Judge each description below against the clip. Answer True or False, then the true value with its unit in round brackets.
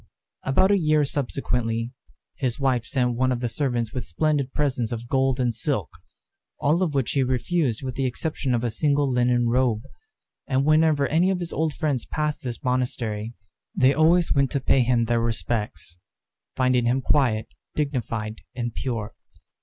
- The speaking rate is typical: True (170 wpm)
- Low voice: True (130 Hz)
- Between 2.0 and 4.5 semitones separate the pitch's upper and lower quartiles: True (3.4 semitones)